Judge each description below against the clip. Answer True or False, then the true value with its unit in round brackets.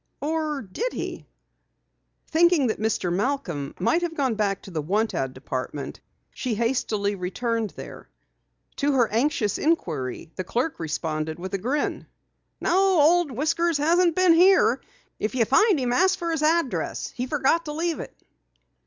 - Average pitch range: False (8.7 semitones)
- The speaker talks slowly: False (155 wpm)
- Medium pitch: False (260 Hz)